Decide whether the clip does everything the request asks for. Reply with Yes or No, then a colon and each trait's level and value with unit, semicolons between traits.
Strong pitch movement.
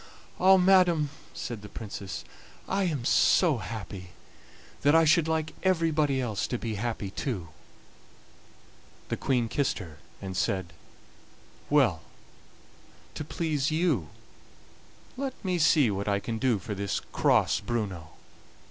Yes: wide, 8.0 semitones